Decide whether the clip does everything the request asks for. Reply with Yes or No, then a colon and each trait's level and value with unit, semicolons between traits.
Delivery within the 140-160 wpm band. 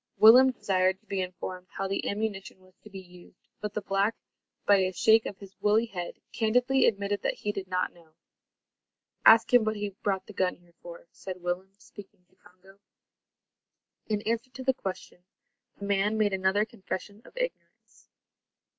No: average, 175 wpm